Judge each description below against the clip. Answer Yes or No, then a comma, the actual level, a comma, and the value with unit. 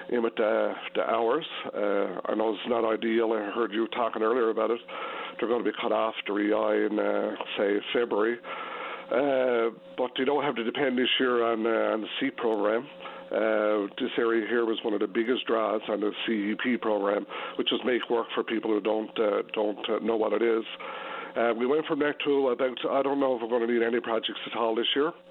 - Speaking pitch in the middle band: No, low, 115 Hz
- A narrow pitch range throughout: Yes, narrow, 2.1 semitones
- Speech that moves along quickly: Yes, fast, 225 wpm